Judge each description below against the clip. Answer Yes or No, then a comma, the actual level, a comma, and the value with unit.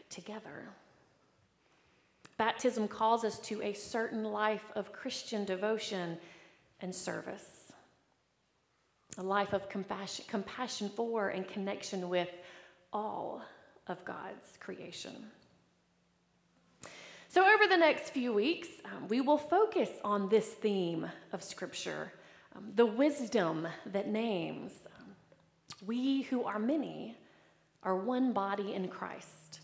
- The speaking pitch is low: No, high, 215 Hz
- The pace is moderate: No, slow, 115 wpm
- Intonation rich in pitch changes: No, average, 3.9 semitones